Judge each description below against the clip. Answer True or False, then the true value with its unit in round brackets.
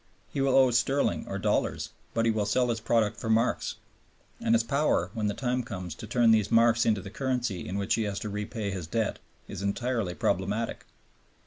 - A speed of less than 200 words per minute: False (205 wpm)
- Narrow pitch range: False (3.2 semitones)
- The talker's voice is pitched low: True (115 Hz)